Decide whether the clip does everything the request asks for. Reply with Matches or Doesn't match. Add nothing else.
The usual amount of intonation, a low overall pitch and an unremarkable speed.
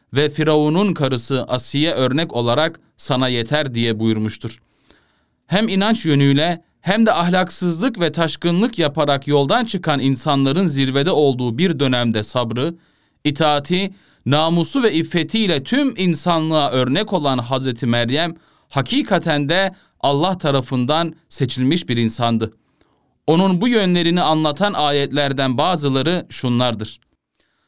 Doesn't match